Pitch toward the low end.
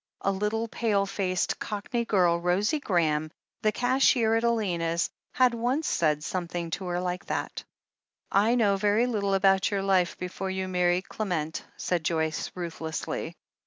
No: high, 190 Hz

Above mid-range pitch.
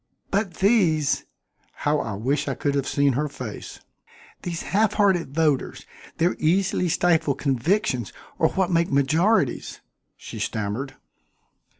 No: medium, 155 Hz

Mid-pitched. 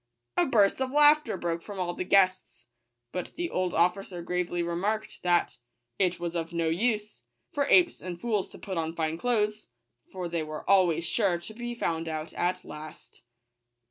Yes: medium, 180 Hz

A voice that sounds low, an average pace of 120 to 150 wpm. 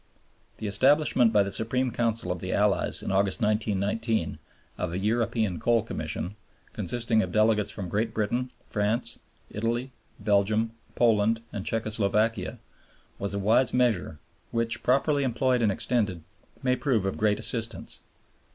Yes: low, 110 Hz; average, 140 wpm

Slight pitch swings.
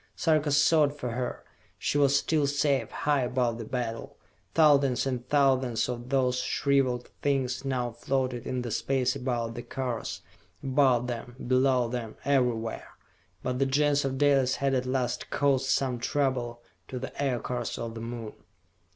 Yes: narrow, 2.3 semitones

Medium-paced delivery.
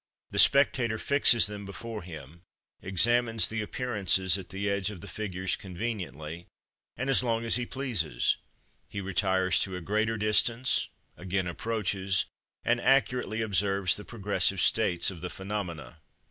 Yes: average, 145 wpm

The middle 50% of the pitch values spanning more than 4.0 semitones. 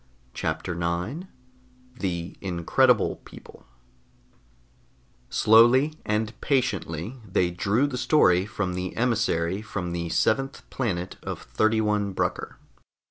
Yes: average, 5.2 semitones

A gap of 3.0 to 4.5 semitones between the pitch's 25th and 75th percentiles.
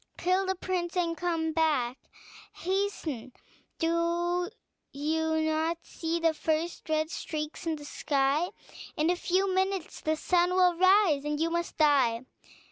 No: narrow, 2.4 semitones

